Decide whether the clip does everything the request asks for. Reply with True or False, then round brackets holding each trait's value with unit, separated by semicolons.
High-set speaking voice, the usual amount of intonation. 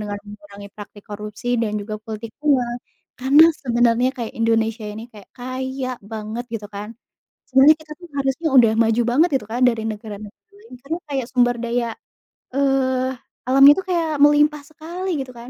True (245 Hz; 3.8 semitones)